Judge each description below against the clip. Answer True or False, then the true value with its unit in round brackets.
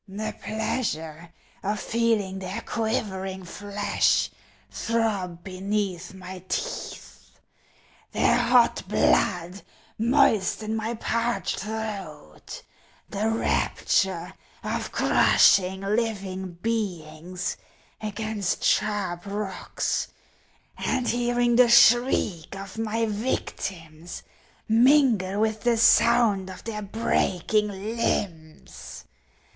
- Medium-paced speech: False (85 wpm)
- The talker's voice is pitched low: False (205 Hz)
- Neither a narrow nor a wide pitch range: True (3.3 semitones)